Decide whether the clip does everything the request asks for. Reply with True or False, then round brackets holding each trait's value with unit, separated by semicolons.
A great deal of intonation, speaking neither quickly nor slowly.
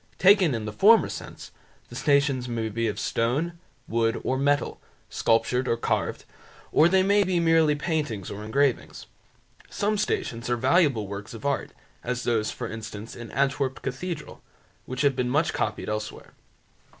True (5.7 semitones; 160 wpm)